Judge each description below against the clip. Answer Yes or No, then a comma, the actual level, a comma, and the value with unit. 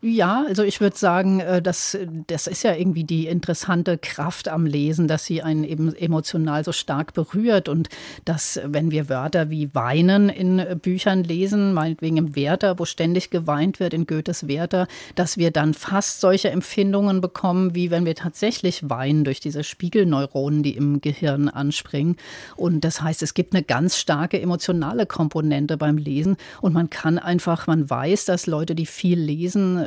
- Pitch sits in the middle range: Yes, medium, 170 Hz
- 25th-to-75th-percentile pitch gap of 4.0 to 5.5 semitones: No, average, 2.9 semitones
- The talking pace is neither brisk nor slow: Yes, average, 170 wpm